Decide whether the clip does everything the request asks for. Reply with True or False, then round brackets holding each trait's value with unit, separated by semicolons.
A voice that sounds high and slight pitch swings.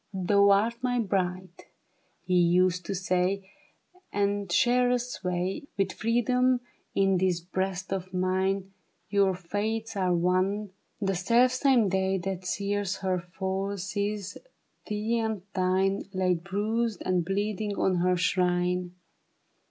True (195 Hz; 2.2 semitones)